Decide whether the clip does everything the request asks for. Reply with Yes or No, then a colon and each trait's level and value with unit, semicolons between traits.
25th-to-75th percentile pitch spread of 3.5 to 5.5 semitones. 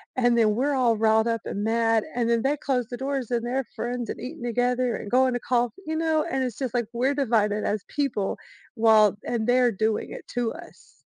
No: narrow, 2.6 semitones